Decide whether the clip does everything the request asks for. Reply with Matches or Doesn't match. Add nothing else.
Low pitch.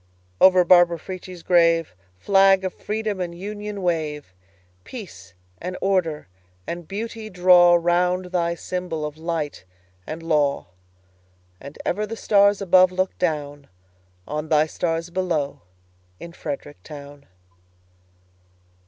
Doesn't match